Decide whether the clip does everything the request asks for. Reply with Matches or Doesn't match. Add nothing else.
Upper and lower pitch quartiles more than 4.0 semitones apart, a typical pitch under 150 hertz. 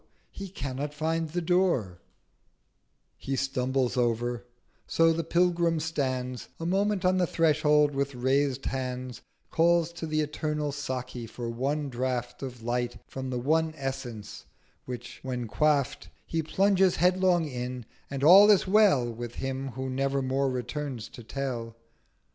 Matches